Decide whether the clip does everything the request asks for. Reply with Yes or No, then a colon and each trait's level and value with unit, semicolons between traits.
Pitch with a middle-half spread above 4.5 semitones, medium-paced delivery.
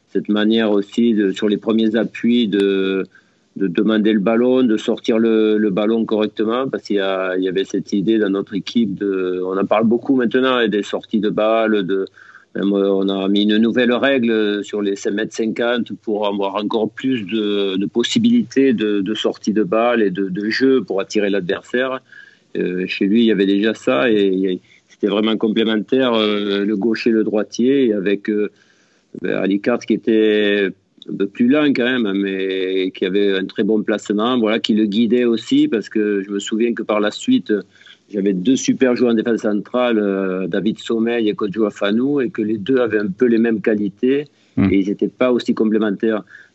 No: narrow, 2.6 semitones; average, 200 wpm